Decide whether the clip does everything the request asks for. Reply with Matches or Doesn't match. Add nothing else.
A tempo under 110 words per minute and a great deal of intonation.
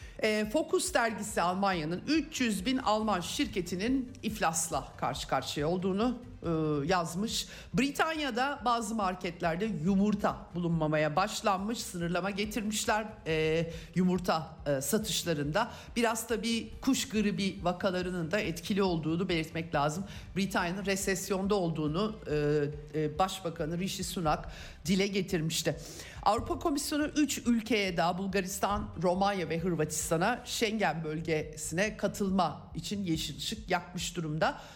Doesn't match